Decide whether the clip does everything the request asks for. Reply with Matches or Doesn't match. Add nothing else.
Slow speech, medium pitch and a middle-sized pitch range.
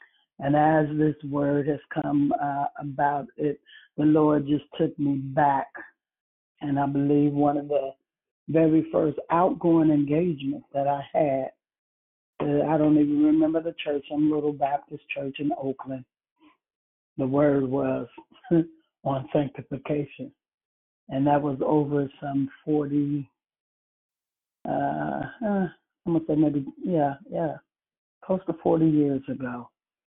Doesn't match